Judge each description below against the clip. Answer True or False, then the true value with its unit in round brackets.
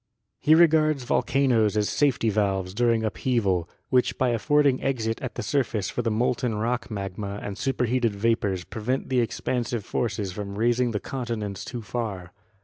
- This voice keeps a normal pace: True (155 wpm)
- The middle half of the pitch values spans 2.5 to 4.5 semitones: True (3.5 semitones)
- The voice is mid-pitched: False (115 Hz)